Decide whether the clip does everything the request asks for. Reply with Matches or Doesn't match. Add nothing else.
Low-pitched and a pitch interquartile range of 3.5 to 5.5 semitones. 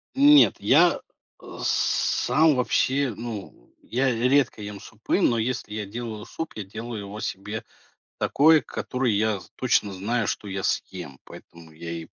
Matches